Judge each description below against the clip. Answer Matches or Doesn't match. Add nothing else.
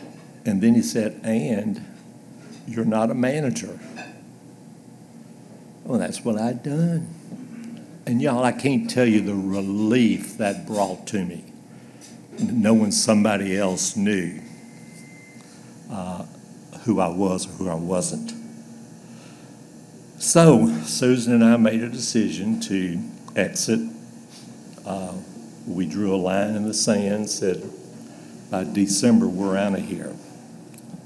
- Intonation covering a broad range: Matches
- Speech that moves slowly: Matches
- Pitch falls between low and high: Doesn't match